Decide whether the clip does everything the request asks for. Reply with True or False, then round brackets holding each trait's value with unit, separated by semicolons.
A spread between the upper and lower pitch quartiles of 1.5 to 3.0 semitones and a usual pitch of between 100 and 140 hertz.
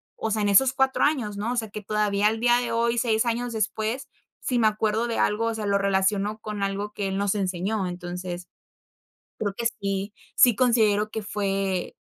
False (2.5 semitones; 210 Hz)